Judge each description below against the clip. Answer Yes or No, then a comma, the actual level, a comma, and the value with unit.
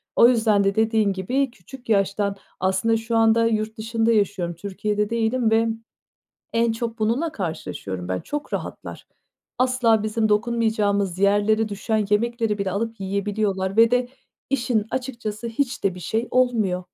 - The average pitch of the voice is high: Yes, high, 220 Hz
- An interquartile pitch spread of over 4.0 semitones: No, narrow, 2.5 semitones